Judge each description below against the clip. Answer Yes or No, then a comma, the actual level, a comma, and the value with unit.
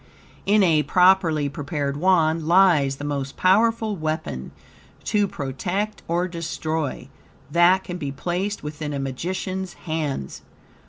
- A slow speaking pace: Yes, slow, 120 wpm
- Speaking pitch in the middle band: Yes, medium, 165 Hz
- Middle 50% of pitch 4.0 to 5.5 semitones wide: Yes, average, 4.3 semitones